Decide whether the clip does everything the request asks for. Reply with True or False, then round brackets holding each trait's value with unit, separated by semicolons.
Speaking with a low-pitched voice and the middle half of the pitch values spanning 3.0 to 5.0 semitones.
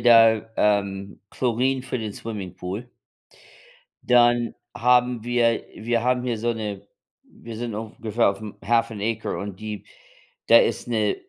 False (115 Hz; 2.4 semitones)